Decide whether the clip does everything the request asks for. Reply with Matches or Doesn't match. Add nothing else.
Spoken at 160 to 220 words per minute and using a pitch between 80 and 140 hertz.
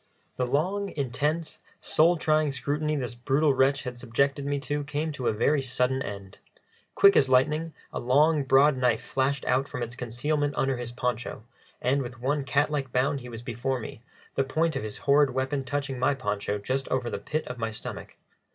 Matches